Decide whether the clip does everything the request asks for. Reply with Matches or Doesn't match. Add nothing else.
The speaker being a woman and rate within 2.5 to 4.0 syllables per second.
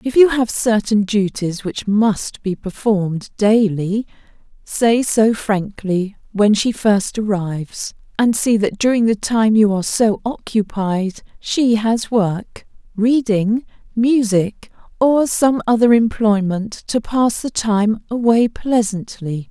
Matches